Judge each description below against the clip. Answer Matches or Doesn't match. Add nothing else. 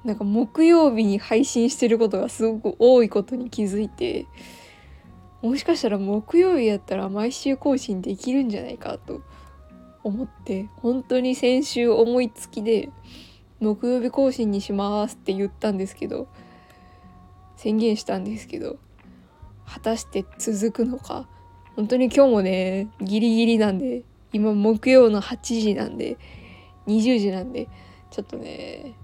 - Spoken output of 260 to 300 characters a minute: Matches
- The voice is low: Doesn't match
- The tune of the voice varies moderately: Matches